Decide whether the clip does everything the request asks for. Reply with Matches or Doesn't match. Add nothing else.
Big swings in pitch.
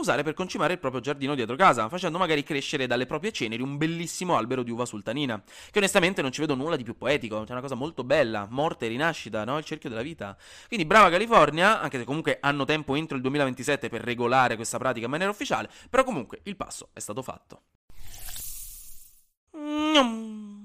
Matches